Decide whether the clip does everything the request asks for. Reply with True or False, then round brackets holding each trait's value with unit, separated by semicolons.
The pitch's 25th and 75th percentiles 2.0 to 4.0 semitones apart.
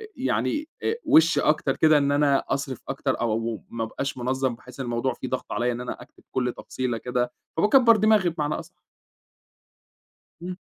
False (4.5 semitones)